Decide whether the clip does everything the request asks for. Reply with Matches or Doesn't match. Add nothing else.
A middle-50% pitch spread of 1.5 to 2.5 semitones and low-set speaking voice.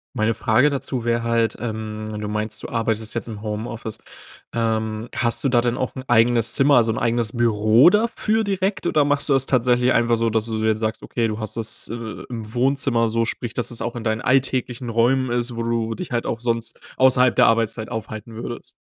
Matches